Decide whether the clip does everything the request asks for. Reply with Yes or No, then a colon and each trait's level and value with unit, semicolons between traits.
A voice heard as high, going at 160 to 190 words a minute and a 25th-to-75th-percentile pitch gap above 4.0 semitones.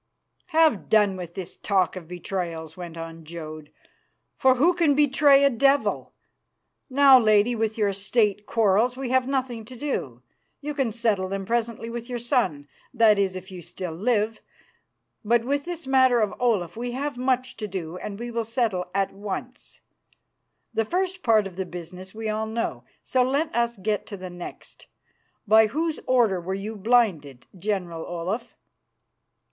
Yes: high, 220 Hz; average, 170 wpm; average, 5.1 semitones